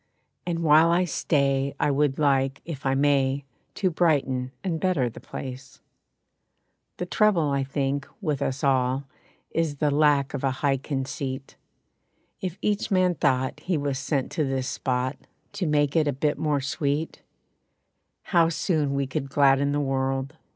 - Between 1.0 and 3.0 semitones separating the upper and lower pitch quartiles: Yes, narrow, 2.6 semitones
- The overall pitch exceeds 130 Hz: Yes, medium, 140 Hz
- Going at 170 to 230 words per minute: No, average, 160 wpm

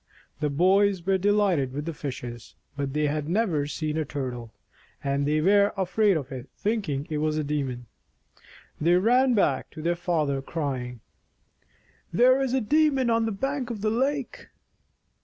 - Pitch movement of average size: No, wide, 7.0 semitones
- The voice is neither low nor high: Yes, medium, 165 Hz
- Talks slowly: No, average, 175 wpm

